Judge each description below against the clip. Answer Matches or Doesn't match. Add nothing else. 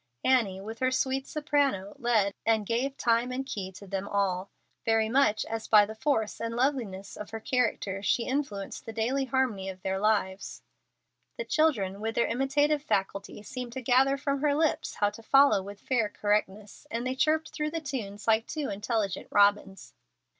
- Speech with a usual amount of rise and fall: Matches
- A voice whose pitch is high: Matches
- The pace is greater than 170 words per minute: Matches